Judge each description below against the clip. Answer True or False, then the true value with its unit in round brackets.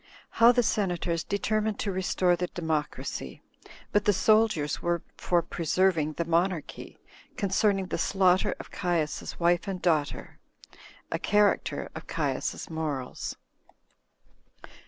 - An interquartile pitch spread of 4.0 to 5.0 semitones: False (3.5 semitones)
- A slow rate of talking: True (115 wpm)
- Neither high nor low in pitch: True (180 Hz)